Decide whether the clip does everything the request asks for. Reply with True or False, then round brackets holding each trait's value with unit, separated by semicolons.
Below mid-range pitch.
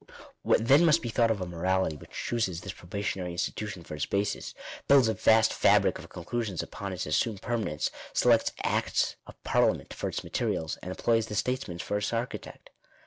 True (105 Hz)